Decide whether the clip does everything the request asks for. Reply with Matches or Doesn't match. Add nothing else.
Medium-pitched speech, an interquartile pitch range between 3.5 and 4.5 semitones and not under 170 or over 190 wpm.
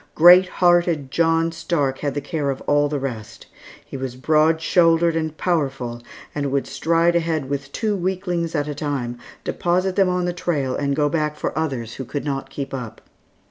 Matches